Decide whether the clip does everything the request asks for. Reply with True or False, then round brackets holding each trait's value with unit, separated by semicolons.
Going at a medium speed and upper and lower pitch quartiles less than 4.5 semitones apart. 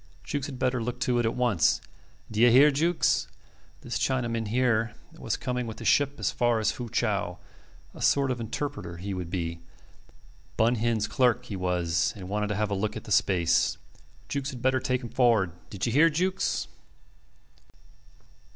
True (175 wpm; 4.0 semitones)